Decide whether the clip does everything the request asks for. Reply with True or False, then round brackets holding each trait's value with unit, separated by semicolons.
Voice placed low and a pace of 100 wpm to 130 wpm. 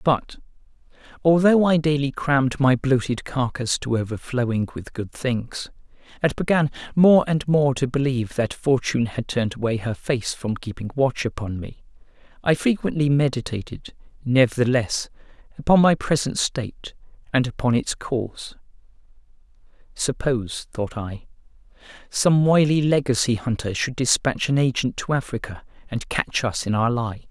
False (130 Hz; 140 wpm)